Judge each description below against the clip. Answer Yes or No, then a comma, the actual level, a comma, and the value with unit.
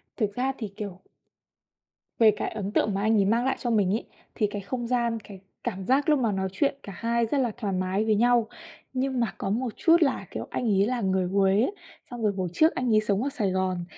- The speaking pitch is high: Yes, high, 220 Hz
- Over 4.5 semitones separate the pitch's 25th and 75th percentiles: No, average, 4.0 semitones